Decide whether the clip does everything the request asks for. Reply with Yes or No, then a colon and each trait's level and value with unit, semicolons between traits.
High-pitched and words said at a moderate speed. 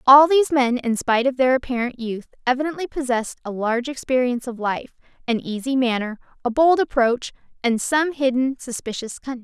Yes: very high, 255 Hz; average, 170 wpm